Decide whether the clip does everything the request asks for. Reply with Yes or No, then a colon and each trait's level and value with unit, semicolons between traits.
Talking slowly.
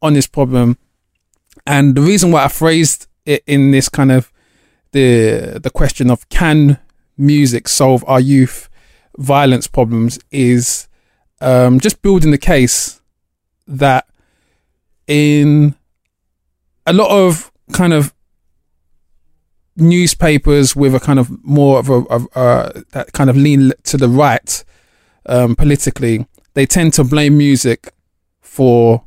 Yes: slow, 130 wpm